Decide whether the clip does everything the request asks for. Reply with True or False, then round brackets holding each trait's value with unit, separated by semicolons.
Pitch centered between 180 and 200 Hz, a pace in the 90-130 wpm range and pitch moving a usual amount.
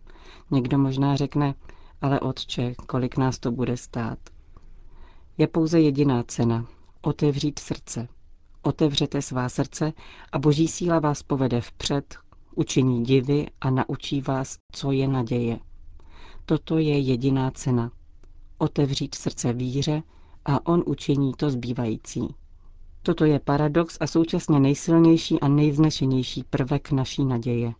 False (140 Hz; 120 wpm; 3.6 semitones)